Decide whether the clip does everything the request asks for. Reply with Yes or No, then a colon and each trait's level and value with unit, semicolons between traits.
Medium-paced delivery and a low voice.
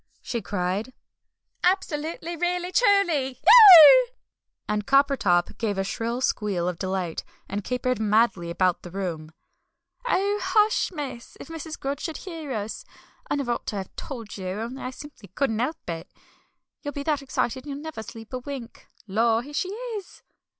No: average, 160 wpm; very high, 255 Hz